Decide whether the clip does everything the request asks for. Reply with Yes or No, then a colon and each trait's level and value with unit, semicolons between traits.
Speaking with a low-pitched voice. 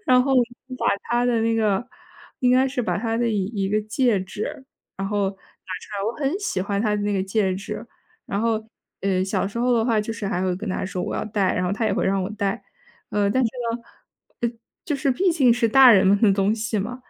No: high, 215 Hz